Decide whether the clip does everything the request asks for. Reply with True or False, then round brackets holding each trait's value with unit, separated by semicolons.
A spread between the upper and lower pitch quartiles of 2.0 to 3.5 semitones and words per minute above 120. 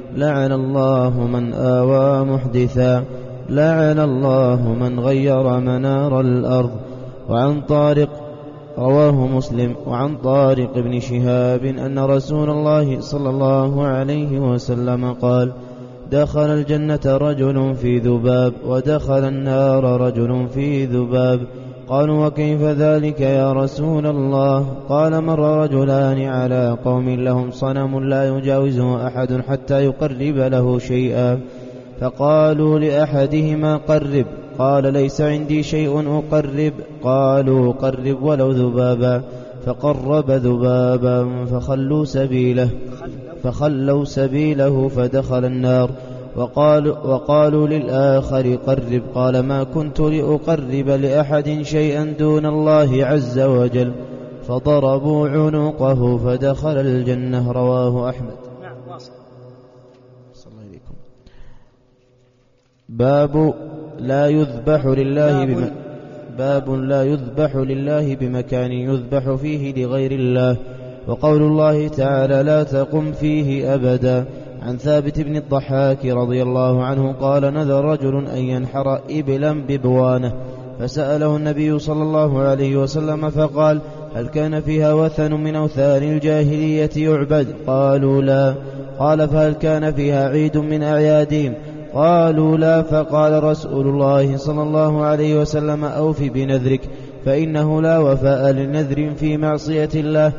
False (2.9 semitones; 105 wpm)